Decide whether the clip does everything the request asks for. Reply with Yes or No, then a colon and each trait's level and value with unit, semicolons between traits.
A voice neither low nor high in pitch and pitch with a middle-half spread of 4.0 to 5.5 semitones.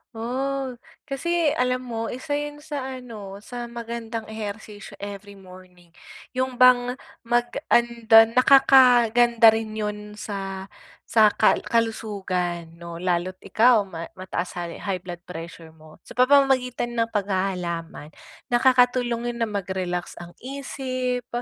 No: high, 225 Hz; average, 4.8 semitones